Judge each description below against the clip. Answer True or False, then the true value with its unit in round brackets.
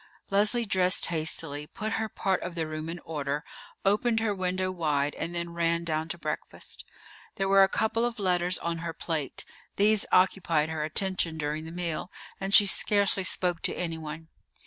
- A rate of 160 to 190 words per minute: True (175 wpm)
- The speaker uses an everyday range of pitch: True (3.4 semitones)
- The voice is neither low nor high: True (175 Hz)